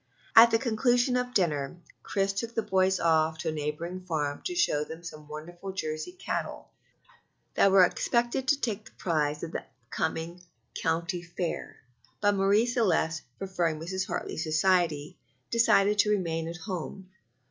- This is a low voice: No, medium, 180 Hz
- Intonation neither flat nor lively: Yes, average, 4.5 semitones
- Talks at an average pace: Yes, average, 155 wpm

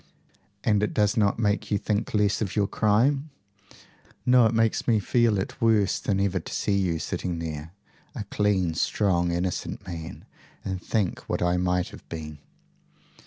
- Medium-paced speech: Yes, average, 165 wpm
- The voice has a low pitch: Yes, low, 100 Hz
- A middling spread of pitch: Yes, average, 3.3 semitones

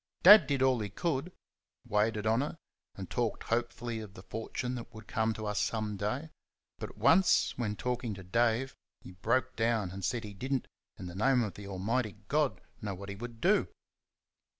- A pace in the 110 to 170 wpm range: No, average, 195 wpm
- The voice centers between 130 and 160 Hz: No, low, 115 Hz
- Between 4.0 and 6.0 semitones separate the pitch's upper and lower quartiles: No, average, 3.6 semitones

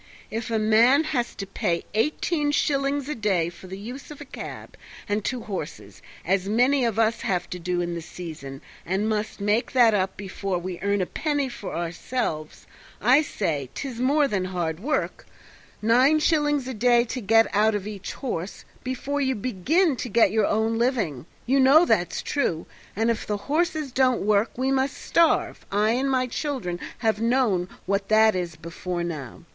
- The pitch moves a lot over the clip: Yes, wide, 5.8 semitones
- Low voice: No, high, 220 Hz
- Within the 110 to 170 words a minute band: No, average, 185 wpm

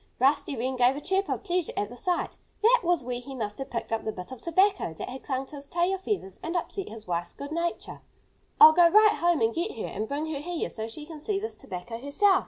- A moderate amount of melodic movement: No, wide, 6.7 semitones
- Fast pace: Yes, fast, 255 wpm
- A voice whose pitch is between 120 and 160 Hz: No, very high, 290 Hz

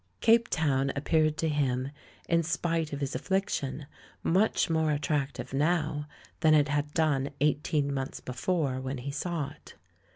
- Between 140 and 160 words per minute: Yes, average, 150 wpm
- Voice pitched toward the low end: No, medium, 150 Hz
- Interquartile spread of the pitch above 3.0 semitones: No, average, 2.7 semitones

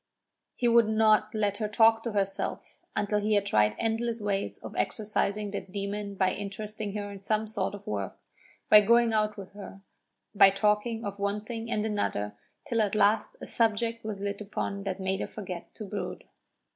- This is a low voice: No, high, 210 Hz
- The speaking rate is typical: Yes, average, 185 wpm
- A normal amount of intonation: No, narrow, 1.6 semitones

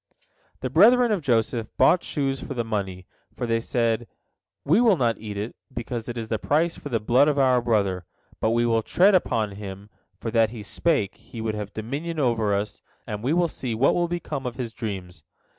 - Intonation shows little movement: No, average, 4.6 semitones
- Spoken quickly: Yes, fast, 210 wpm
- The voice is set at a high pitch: No, low, 120 Hz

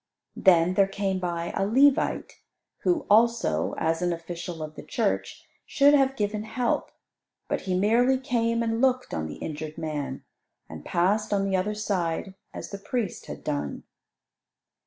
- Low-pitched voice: No, high, 200 Hz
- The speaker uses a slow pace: No, average, 155 wpm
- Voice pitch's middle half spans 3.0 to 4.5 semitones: No, average, 5.2 semitones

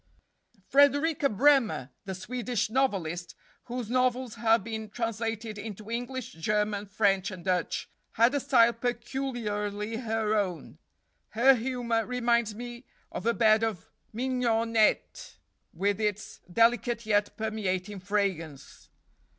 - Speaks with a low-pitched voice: No, high, 225 Hz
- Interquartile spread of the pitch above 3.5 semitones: No, average, 2.9 semitones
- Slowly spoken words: Yes, slow, 115 wpm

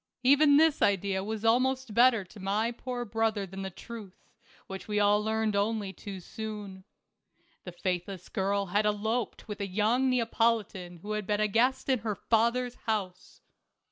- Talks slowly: No, average, 165 wpm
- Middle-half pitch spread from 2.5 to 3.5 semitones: Yes, average, 2.9 semitones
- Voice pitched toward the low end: No, high, 215 Hz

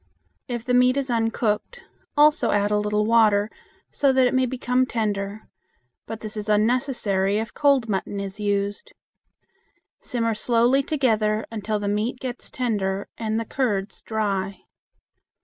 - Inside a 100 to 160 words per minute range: Yes, average, 145 wpm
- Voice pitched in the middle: No, high, 220 Hz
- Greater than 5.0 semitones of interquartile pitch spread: No, average, 3.3 semitones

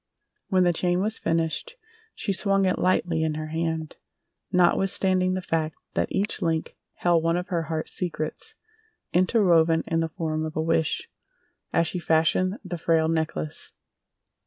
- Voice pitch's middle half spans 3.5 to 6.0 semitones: No, narrow, 2.4 semitones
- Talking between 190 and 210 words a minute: No, average, 155 wpm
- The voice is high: No, medium, 165 Hz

